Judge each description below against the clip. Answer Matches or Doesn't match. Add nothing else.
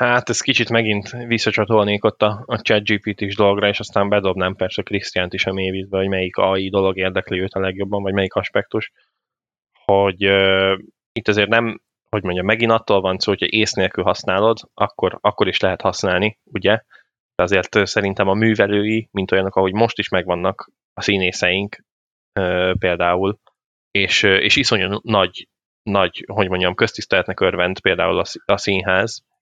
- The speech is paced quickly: Matches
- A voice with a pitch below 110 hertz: Matches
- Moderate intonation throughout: Doesn't match